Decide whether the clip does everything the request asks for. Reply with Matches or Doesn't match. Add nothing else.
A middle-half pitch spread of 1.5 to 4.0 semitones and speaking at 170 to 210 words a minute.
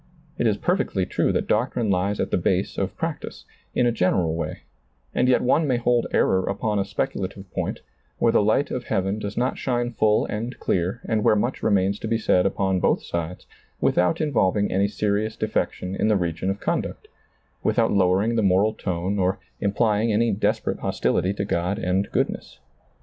Matches